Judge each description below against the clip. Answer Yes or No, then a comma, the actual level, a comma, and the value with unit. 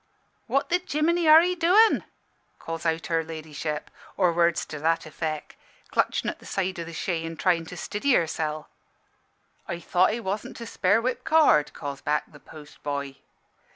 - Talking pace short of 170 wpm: No, average, 175 wpm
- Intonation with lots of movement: Yes, wide, 7.2 semitones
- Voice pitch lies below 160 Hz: No, medium, 170 Hz